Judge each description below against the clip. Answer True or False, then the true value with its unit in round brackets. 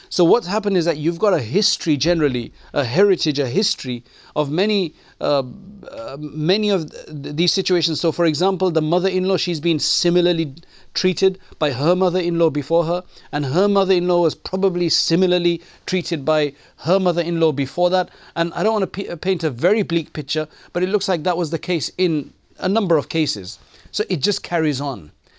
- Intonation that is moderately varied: True (3.3 semitones)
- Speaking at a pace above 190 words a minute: False (185 wpm)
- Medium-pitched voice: True (170 Hz)